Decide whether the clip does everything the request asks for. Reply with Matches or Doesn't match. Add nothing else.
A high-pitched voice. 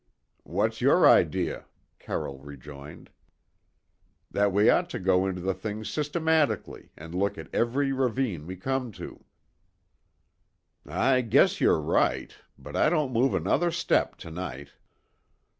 Doesn't match